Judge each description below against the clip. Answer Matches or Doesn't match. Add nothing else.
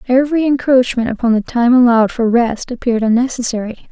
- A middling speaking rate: Matches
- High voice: Matches